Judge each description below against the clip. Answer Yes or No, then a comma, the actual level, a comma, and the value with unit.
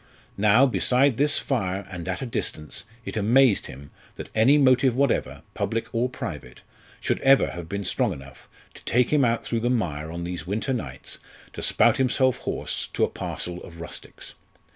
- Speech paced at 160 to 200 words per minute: Yes, average, 180 wpm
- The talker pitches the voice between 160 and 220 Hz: No, low, 115 Hz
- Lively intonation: Yes, wide, 6.5 semitones